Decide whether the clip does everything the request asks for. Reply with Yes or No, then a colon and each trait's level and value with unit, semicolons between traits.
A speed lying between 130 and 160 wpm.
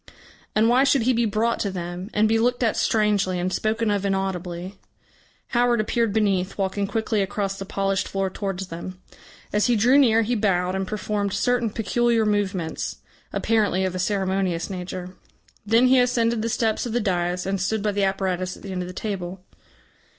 No: average, 185 wpm